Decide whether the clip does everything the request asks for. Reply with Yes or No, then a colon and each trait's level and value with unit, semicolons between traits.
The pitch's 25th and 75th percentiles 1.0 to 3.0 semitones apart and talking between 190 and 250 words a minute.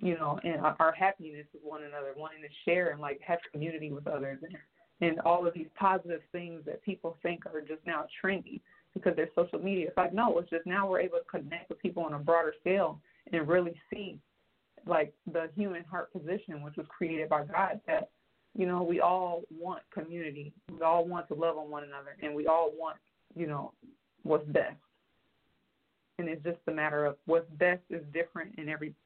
Yes: narrow, 2.4 semitones; average, 200 wpm